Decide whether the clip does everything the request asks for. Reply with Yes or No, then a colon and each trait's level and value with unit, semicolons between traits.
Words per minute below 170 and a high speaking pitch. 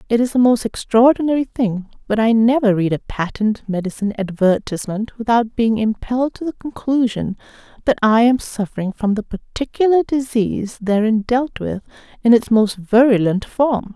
Yes: average, 155 wpm; high, 225 Hz